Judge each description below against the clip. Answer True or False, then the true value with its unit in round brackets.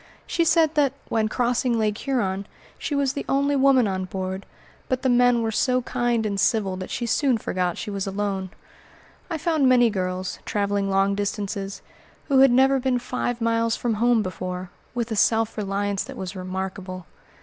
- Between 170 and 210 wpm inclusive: True (180 wpm)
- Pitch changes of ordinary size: True (4.5 semitones)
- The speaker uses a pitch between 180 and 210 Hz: False (220 Hz)